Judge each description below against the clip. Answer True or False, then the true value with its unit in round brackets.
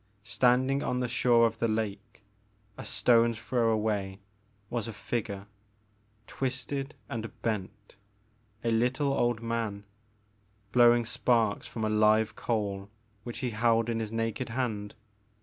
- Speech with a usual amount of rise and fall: False (2.0 semitones)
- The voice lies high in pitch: False (115 Hz)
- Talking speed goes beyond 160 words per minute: False (135 wpm)